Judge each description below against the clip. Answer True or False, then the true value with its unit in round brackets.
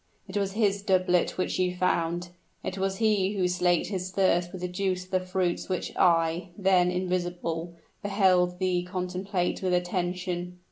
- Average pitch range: False (1.1 semitones)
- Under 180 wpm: True (160 wpm)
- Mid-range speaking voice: True (180 Hz)